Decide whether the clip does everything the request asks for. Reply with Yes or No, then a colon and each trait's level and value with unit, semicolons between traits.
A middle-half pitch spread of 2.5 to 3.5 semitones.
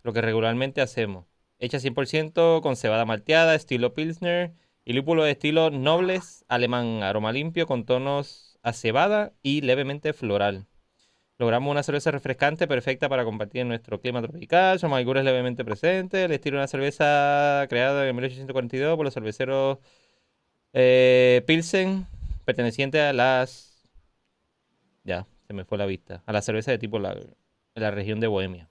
No: average, 4.4 semitones